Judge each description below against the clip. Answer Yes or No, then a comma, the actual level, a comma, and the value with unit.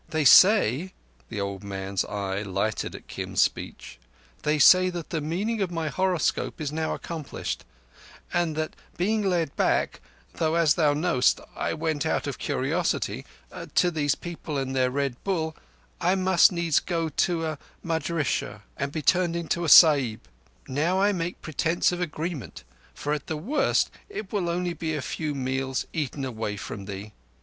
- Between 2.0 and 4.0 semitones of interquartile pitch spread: No, average, 4.6 semitones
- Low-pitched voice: No, medium, 155 Hz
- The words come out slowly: No, average, 160 wpm